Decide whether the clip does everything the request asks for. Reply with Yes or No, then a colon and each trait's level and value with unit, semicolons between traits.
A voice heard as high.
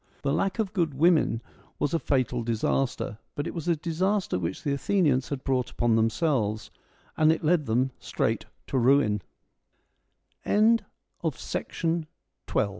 No: medium, 140 Hz